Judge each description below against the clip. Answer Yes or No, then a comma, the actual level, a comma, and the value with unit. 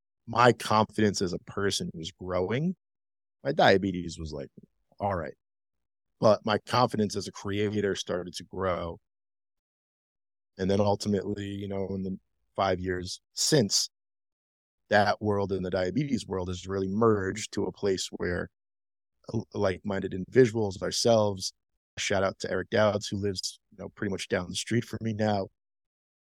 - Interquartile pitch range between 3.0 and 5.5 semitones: No, narrow, 2.5 semitones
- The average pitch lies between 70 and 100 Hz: Yes, very low, 95 Hz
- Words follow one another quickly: No, average, 150 wpm